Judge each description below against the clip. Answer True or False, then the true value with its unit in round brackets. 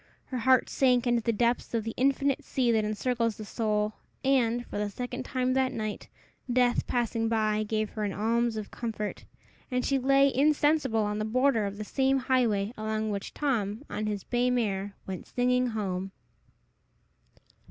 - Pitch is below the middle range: False (230 Hz)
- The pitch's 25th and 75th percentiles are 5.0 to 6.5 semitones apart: False (3.0 semitones)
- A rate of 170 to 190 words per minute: True (175 wpm)